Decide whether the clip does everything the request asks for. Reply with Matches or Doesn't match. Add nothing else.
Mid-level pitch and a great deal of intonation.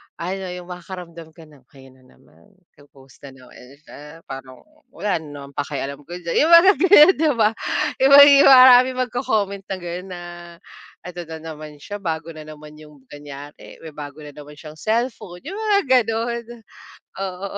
Matches